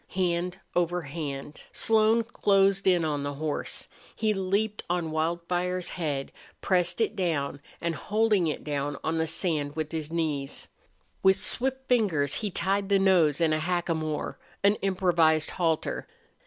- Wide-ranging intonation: No, average, 3.7 semitones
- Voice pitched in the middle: Yes, medium, 175 Hz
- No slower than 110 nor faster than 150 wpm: Yes, average, 145 wpm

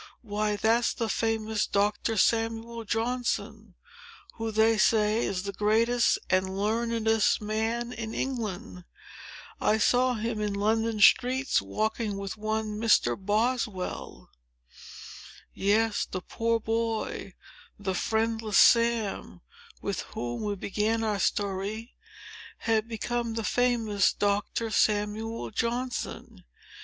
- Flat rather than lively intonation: Yes, narrow, 1.8 semitones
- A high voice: Yes, high, 220 Hz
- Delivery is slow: Yes, slow, 105 wpm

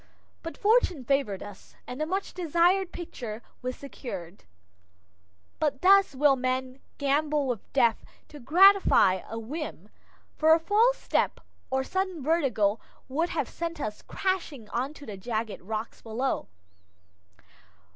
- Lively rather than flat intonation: Yes, wide, 6.3 semitones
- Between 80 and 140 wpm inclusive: Yes, slow, 135 wpm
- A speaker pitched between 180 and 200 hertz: No, very high, 275 Hz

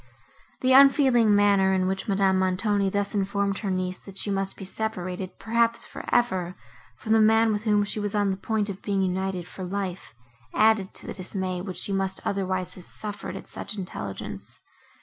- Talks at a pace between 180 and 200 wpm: Yes, average, 190 wpm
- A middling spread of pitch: No, narrow, 2.2 semitones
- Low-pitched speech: No, high, 195 Hz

